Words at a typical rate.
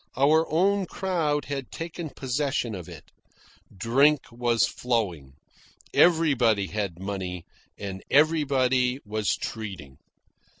No: slow, 100 wpm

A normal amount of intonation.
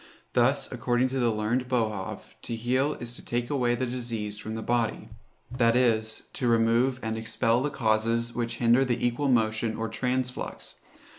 No: narrow, 2.0 semitones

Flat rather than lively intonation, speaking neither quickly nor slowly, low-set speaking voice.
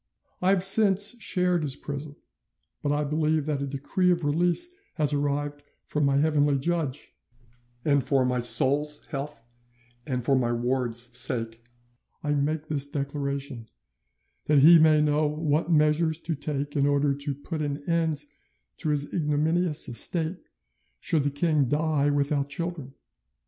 No: narrow, 2.2 semitones; average, 150 wpm; medium, 145 Hz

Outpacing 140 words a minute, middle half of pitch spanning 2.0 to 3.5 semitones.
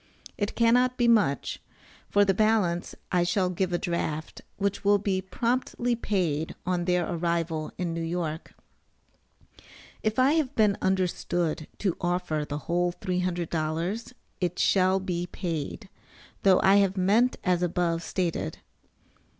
No: slow, 135 wpm; average, 3.0 semitones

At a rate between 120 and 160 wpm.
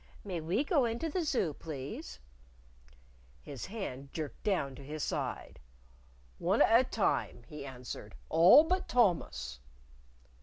Yes: average, 140 wpm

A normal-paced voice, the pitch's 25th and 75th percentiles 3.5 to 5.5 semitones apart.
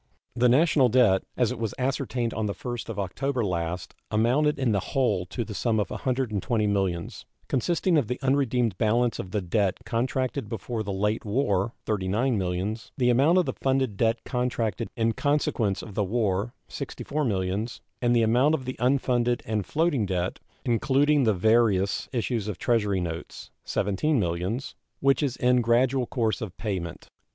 Yes: average, 170 wpm; average, 4.1 semitones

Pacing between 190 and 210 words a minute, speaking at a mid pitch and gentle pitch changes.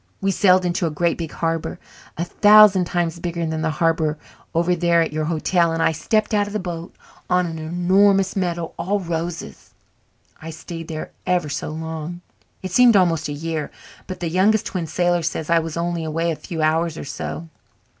Yes: average, 195 wpm; medium, 170 Hz; narrow, 2.0 semitones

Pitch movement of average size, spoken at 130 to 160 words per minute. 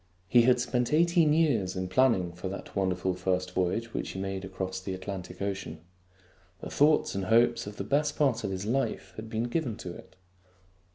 No: average, 4.9 semitones; average, 190 wpm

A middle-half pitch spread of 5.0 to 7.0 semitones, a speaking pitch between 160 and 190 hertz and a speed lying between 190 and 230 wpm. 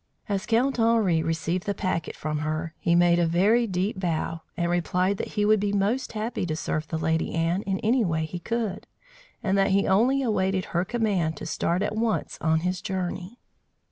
No: average, 4.3 semitones; medium, 185 Hz; average, 200 wpm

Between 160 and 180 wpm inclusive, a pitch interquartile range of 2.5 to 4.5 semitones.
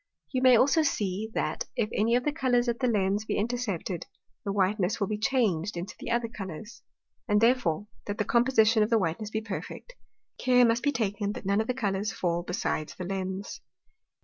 No: average, 195 wpm; average, 3.8 semitones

